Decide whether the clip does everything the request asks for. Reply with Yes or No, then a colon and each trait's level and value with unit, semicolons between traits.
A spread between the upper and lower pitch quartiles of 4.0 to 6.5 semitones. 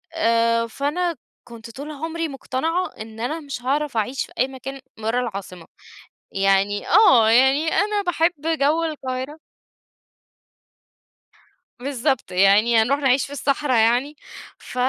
Yes: average, 4.6 semitones